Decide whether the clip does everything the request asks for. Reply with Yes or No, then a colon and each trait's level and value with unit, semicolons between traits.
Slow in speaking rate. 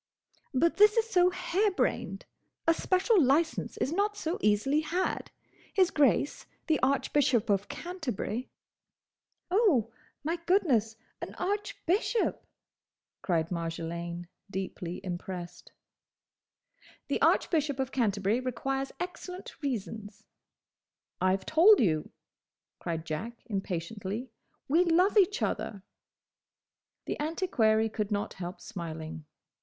Yes: slow, 105 wpm